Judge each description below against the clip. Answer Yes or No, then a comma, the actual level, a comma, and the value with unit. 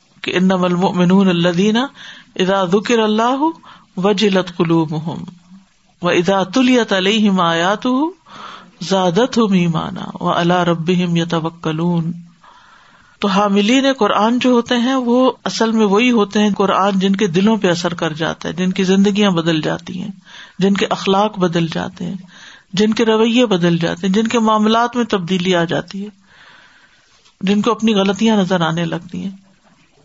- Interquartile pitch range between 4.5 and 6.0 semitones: No, average, 3.1 semitones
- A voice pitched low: No, high, 195 Hz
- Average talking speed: Yes, average, 150 wpm